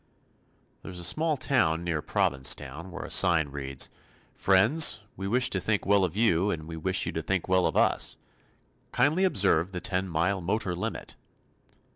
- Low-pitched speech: Yes, very low, 95 Hz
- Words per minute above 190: No, average, 175 wpm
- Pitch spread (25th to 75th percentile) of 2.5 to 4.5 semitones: Yes, average, 3.9 semitones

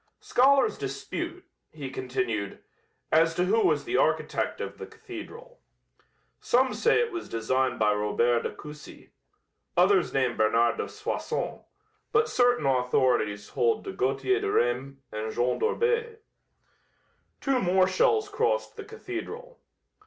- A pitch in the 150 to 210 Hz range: Yes, high, 190 Hz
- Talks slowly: Yes, slow, 130 wpm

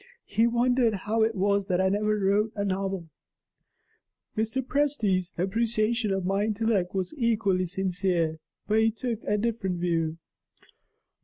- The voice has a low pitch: No, high, 205 Hz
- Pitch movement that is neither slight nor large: Yes, average, 3.0 semitones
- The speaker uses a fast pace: No, average, 140 wpm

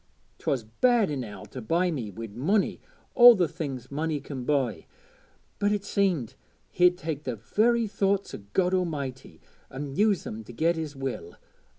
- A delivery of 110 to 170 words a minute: Yes, average, 165 wpm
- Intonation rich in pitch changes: Yes, wide, 7.1 semitones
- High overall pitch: No, medium, 150 Hz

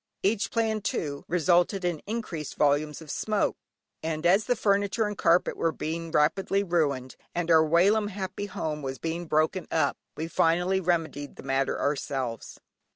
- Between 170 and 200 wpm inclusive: No, average, 155 wpm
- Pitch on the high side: No, medium, 170 Hz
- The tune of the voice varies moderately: Yes, average, 4.3 semitones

